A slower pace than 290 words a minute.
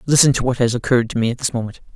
No: fast, 305 wpm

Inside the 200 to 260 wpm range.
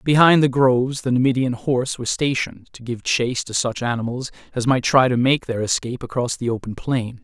Yes: fast, 205 wpm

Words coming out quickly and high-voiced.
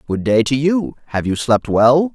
No: fast, 225 wpm; low, 135 Hz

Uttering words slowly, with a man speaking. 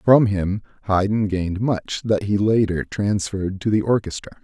No: average, 160 wpm; male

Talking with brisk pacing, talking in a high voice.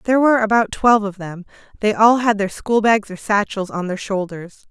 Yes: fast, 215 wpm; high, 210 Hz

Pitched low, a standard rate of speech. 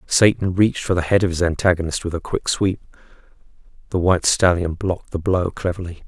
Yes: very low, 90 Hz; average, 190 wpm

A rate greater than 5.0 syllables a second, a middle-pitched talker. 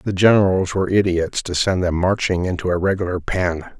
No: 5.5 syllables/s; very low, 90 Hz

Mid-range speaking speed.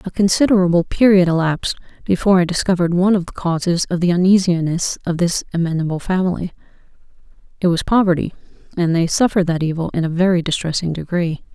Yes: average, 160 wpm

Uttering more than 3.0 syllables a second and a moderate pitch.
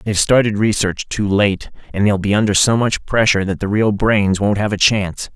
No: 5.4 syllables/s; low, 105 Hz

